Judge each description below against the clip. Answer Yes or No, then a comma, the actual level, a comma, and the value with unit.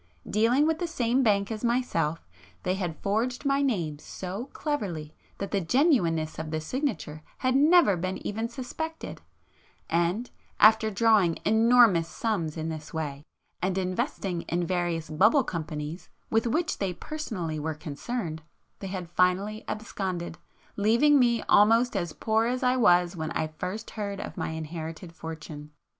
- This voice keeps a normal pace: Yes, average, 150 wpm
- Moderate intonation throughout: No, wide, 6.2 semitones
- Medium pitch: No, high, 195 Hz